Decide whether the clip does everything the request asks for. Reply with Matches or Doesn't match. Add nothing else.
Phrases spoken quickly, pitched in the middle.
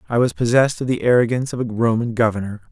Doesn't match